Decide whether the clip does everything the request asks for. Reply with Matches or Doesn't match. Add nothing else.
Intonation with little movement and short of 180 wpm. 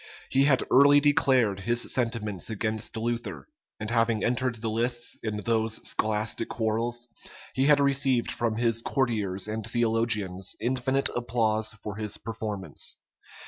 Matches